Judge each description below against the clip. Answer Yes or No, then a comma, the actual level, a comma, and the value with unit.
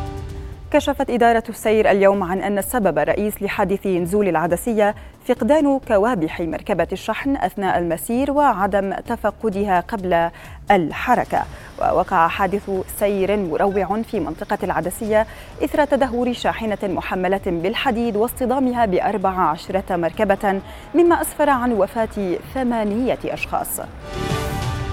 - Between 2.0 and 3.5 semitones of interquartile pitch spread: No, average, 3.9 semitones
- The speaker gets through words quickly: No, average, 105 wpm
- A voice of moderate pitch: No, high, 205 Hz